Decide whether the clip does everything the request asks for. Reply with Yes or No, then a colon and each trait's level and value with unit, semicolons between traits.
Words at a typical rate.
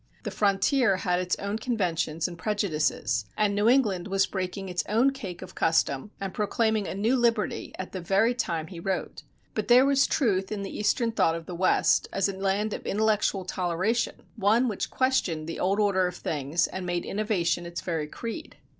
Yes: average, 190 wpm